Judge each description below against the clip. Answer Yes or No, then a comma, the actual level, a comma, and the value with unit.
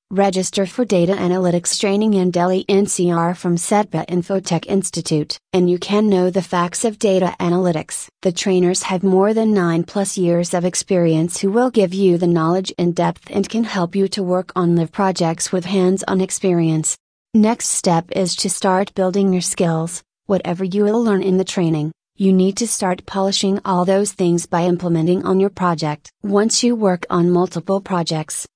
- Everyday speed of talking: Yes, average, 180 wpm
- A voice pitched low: No, medium, 185 Hz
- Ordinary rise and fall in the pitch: No, narrow, 2.0 semitones